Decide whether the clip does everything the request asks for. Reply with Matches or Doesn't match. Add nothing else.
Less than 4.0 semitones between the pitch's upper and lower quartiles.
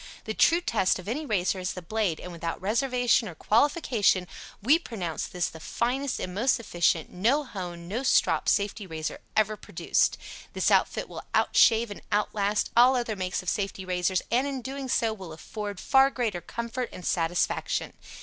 Doesn't match